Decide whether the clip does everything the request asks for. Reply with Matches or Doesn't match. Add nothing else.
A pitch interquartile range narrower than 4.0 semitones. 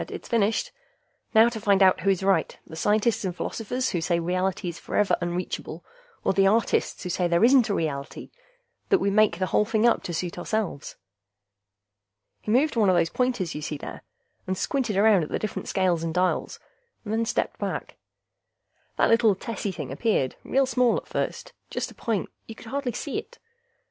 Doesn't match